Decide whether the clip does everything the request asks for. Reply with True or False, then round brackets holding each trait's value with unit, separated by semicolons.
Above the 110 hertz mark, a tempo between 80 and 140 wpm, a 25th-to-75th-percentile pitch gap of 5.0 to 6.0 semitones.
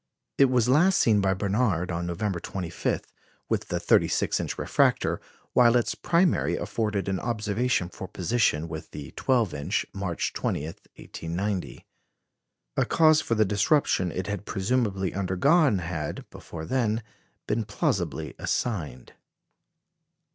False (100 Hz; 135 wpm; 5.4 semitones)